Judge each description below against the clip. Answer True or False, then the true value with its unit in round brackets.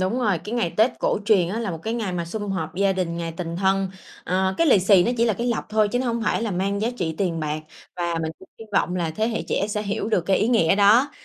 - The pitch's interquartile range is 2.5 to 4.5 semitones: True (3.9 semitones)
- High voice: True (195 Hz)